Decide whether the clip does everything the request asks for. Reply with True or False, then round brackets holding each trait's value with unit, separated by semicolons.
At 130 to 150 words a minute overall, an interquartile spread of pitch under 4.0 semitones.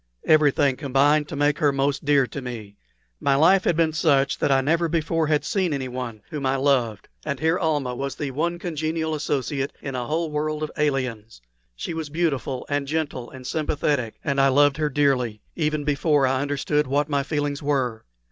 False (190 wpm; 2.4 semitones)